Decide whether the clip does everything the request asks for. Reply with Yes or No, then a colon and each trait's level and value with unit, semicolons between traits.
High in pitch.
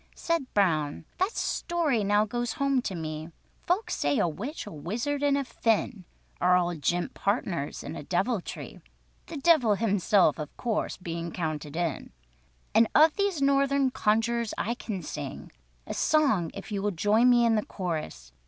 Yes: high, 210 Hz